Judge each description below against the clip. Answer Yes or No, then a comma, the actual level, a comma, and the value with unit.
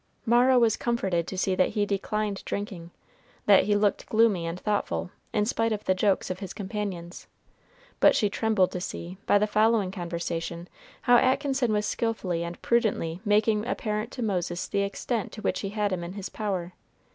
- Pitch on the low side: No, high, 205 Hz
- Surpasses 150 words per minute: Yes, average, 180 wpm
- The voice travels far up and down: No, average, 3.2 semitones